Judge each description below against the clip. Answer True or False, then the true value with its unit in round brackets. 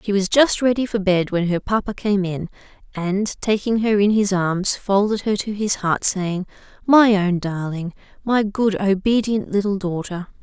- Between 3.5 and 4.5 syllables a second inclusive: True (4.4 syllables/s)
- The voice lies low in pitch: False (200 Hz)